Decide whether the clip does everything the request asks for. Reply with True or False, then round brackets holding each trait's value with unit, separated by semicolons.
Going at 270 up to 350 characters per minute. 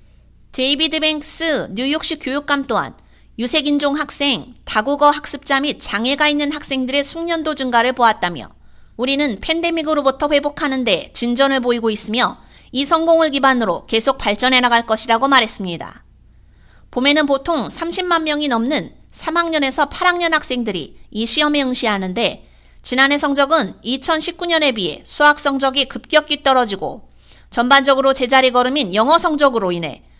True (325 characters per minute)